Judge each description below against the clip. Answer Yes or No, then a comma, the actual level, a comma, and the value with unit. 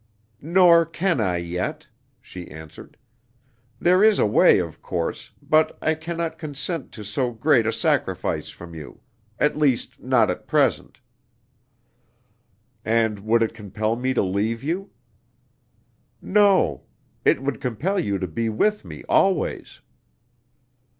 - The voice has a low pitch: Yes, low, 120 Hz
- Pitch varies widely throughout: Yes, wide, 8.1 semitones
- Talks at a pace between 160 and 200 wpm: No, slow, 135 wpm